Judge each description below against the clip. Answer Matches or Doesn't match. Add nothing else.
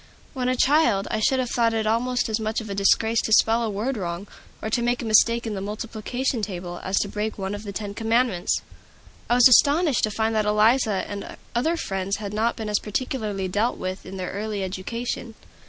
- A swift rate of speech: Matches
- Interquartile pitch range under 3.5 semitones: Matches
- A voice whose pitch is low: Doesn't match